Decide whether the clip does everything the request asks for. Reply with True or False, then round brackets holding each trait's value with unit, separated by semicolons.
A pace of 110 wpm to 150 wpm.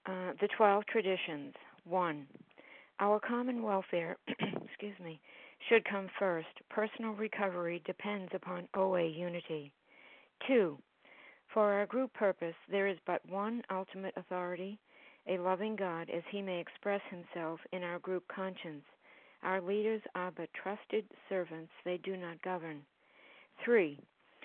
True (135 wpm)